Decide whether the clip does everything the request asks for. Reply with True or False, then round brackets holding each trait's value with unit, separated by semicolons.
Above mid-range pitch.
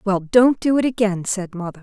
True (205 Hz)